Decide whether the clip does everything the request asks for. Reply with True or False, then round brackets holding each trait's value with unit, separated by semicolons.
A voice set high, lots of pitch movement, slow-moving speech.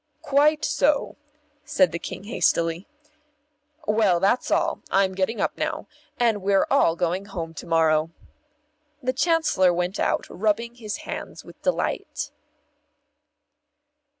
True (200 Hz; 6.5 semitones; 125 wpm)